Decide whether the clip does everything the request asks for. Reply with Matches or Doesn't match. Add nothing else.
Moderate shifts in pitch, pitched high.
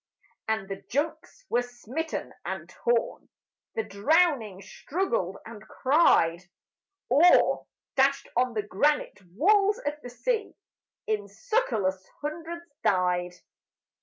Doesn't match